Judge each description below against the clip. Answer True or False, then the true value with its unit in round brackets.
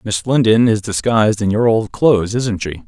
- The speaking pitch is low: True (110 Hz)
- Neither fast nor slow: False (210 wpm)